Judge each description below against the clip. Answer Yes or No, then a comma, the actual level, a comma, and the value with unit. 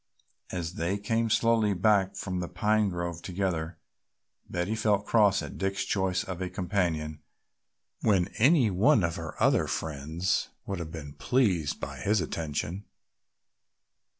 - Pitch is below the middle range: Yes, very low, 95 Hz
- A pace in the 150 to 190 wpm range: No, average, 140 wpm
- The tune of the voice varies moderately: Yes, average, 3.5 semitones